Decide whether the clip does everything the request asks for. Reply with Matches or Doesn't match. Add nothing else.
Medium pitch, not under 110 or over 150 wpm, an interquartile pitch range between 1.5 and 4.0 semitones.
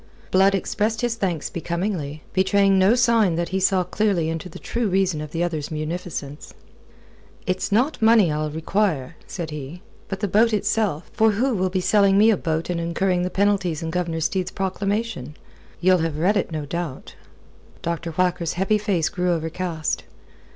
Doesn't match